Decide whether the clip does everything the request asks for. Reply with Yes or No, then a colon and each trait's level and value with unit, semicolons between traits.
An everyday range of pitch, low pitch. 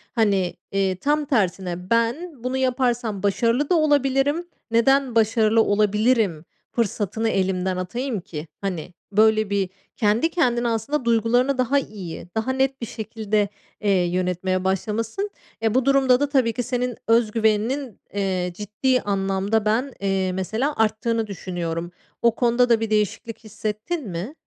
No: average, 4.3 semitones; high, 220 Hz